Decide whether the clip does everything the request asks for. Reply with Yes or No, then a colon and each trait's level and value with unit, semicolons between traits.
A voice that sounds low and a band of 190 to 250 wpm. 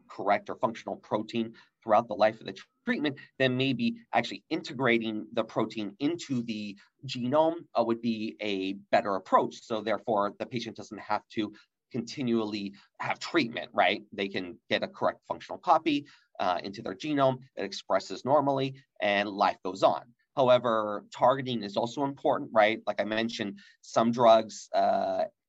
No: low, 120 Hz; average, 155 wpm